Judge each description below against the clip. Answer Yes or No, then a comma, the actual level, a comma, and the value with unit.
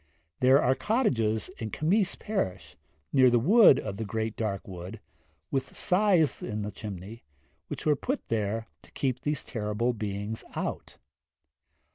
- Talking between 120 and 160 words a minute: Yes, average, 145 wpm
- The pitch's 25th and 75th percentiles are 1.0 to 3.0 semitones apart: No, wide, 5.4 semitones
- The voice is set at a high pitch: No, low, 115 Hz